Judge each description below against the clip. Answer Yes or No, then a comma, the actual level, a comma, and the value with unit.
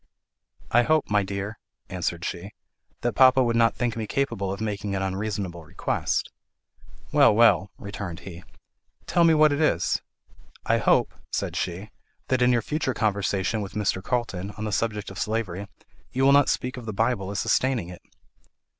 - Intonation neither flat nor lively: Yes, average, 4.0 semitones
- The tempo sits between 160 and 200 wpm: Yes, average, 170 wpm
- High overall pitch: No, low, 105 Hz